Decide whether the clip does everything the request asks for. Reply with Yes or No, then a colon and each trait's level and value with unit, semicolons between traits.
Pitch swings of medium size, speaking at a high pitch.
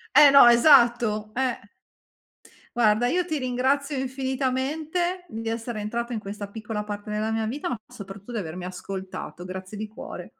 Yes: average, 4.0 semitones; high, 235 Hz